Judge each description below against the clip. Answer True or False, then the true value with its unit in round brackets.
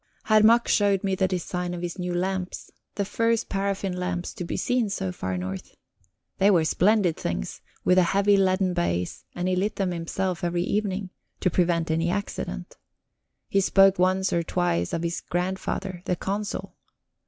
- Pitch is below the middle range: False (185 Hz)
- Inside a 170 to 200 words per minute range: True (175 wpm)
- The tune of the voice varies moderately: False (2.2 semitones)